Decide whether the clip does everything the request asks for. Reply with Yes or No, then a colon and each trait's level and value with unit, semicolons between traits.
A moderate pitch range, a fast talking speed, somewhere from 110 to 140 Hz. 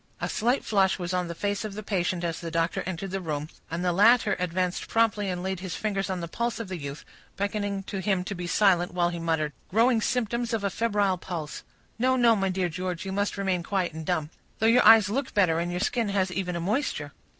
No: average, 3.2 semitones; fast, 235 wpm; high, 190 Hz